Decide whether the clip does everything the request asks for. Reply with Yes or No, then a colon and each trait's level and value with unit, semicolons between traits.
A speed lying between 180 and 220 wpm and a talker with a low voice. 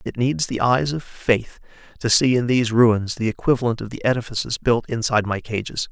Yes: fast, 205 wpm; low, 120 Hz